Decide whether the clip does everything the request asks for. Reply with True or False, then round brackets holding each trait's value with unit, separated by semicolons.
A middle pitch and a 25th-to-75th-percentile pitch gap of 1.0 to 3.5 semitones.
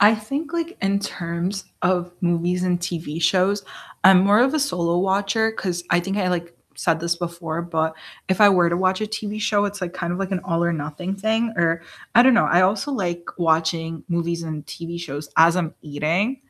True (180 Hz; 3.1 semitones)